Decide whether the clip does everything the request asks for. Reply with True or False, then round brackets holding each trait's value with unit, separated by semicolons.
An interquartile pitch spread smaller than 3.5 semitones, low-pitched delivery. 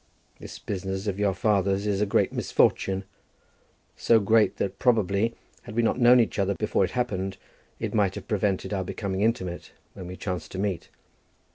True (2.4 semitones; 100 Hz)